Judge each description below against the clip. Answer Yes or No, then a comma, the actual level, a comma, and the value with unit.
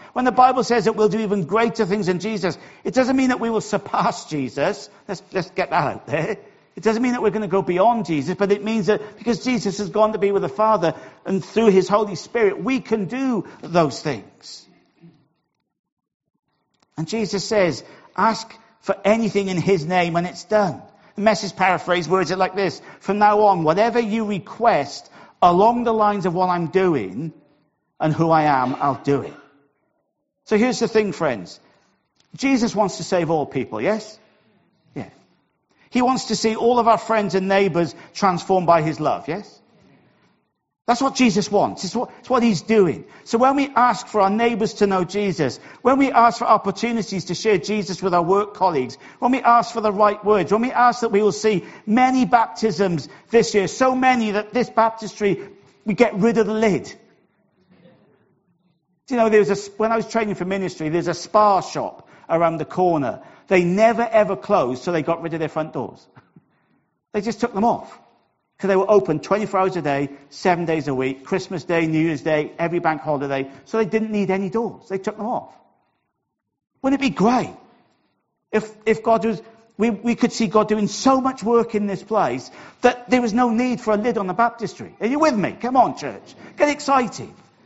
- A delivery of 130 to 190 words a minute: No, average, 200 wpm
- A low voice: No, high, 205 Hz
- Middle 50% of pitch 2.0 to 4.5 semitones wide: Yes, average, 4.1 semitones